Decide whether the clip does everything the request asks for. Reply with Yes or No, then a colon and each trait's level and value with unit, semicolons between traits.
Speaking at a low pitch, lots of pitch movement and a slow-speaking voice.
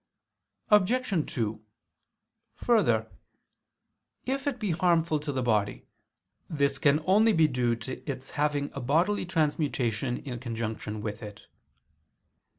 No: medium, 145 Hz; wide, 6.9 semitones; slow, 120 wpm